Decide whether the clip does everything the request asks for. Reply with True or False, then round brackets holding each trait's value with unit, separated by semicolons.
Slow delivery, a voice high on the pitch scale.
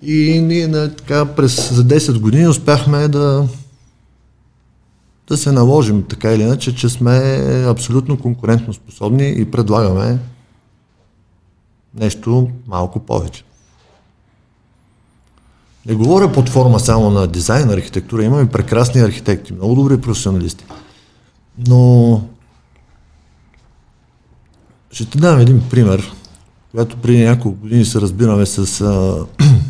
False (105 wpm; 115 Hz)